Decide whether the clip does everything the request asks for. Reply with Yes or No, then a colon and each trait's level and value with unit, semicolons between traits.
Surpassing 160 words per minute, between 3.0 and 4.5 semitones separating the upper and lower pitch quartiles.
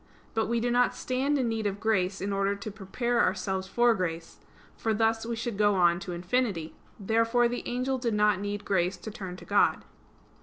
Yes: average, 200 wpm; average, 3.7 semitones